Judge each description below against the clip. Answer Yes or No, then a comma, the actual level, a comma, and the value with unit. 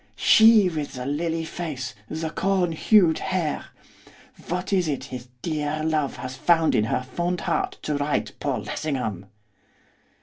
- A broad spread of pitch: No, average, 3.8 semitones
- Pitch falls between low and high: Yes, medium, 155 Hz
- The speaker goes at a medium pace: Yes, average, 145 wpm